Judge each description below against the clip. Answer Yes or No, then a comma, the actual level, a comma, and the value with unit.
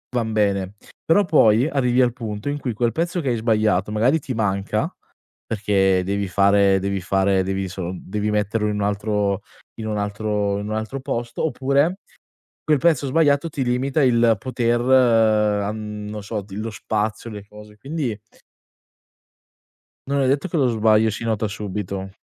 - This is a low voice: Yes, low, 110 Hz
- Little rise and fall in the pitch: No, average, 3.6 semitones